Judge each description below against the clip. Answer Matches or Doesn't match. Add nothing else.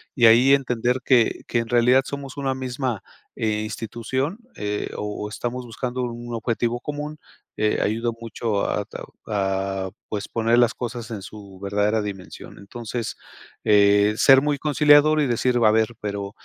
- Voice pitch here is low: Matches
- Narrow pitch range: Doesn't match